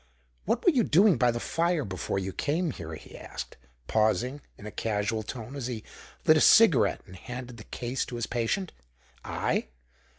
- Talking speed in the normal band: Yes, average, 185 wpm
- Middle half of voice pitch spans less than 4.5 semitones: No, wide, 5.4 semitones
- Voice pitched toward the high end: No, low, 120 Hz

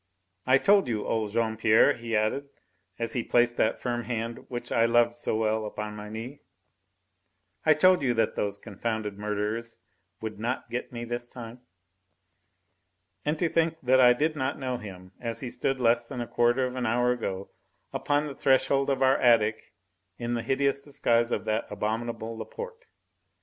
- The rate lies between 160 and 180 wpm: Yes, average, 175 wpm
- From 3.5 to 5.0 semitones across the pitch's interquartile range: No, average, 2.9 semitones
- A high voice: No, low, 120 Hz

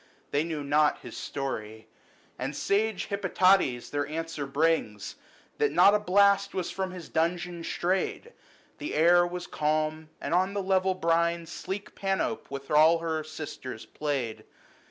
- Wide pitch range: No, average, 4.0 semitones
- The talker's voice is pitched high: No, medium, 165 Hz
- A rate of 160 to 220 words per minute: No, average, 150 wpm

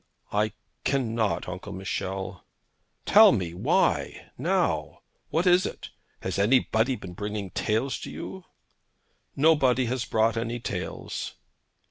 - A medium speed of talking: No, slow, 120 wpm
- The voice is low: Yes, low, 110 Hz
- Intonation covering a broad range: No, average, 4.9 semitones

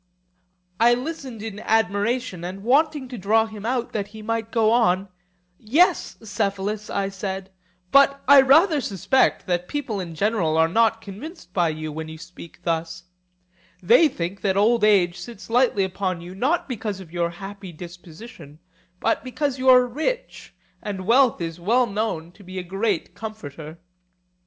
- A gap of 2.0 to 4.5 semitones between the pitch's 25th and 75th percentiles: No, average, 5.1 semitones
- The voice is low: No, high, 205 Hz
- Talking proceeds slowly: No, average, 160 wpm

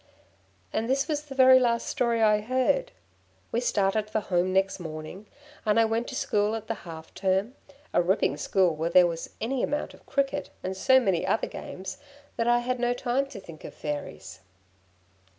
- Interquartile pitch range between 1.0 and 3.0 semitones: No, wide, 5.5 semitones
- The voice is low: No, high, 215 Hz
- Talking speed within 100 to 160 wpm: No, average, 190 wpm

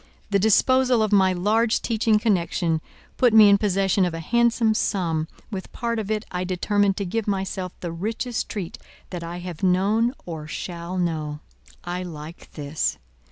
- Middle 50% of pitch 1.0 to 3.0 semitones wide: No, average, 4.0 semitones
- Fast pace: No, average, 165 wpm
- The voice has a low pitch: No, high, 190 Hz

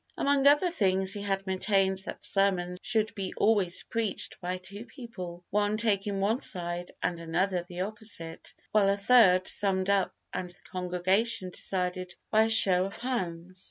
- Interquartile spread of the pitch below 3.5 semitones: Yes, average, 2.9 semitones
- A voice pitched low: No, high, 195 Hz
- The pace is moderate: Yes, average, 160 wpm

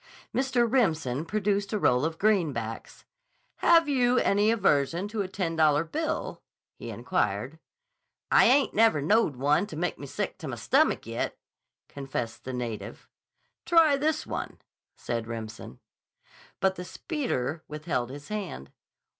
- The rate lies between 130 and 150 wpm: Yes, average, 140 wpm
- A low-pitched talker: No, medium, 175 Hz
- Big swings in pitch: Yes, wide, 8.4 semitones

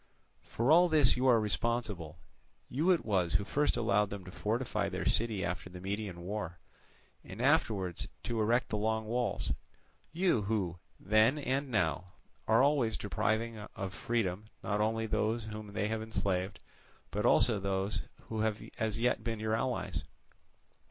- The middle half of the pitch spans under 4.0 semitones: Yes, average, 2.9 semitones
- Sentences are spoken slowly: No, average, 155 wpm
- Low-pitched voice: Yes, low, 110 Hz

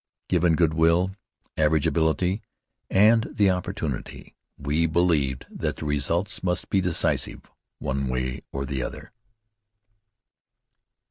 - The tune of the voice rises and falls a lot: No, average, 4.2 semitones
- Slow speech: Yes, slow, 115 wpm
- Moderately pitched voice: No, very low, 80 Hz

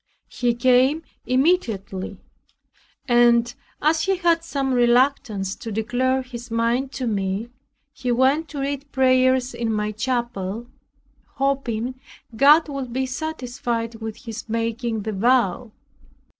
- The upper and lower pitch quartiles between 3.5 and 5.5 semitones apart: No, average, 2.7 semitones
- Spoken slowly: Yes, slow, 120 wpm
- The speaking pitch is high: Yes, high, 245 Hz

